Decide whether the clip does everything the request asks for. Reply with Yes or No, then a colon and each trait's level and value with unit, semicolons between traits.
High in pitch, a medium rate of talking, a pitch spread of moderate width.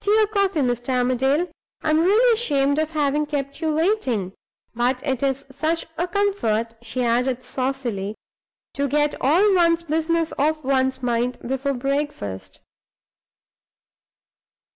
No: very high, 280 Hz; slow, 130 wpm; average, 4.4 semitones